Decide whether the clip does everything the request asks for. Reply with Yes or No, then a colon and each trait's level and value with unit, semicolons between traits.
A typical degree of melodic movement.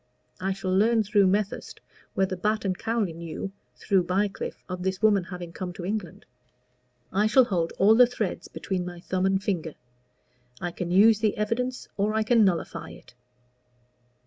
Yes: average, 3.0 semitones